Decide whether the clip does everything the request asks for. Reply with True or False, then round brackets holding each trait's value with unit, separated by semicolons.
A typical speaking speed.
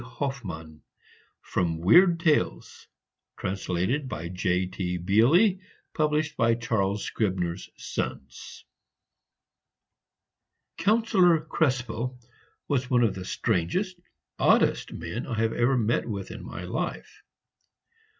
False (95 wpm)